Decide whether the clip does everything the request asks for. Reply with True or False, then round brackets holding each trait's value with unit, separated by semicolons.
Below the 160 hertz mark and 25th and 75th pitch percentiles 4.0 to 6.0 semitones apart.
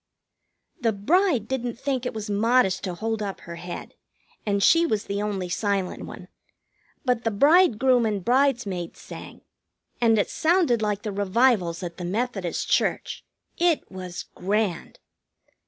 False (215 Hz; 4.4 semitones)